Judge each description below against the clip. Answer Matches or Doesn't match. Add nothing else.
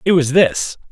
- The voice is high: Doesn't match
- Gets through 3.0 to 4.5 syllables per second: Matches